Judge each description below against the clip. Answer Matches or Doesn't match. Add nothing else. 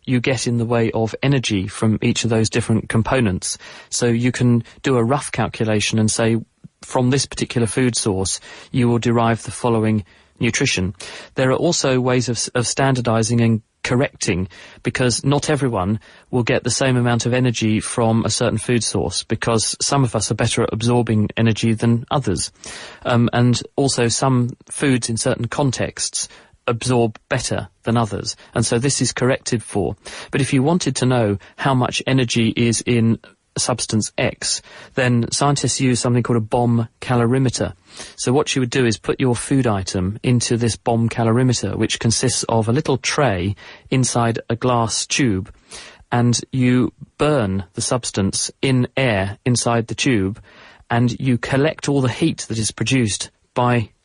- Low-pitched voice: Matches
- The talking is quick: Doesn't match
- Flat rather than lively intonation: Matches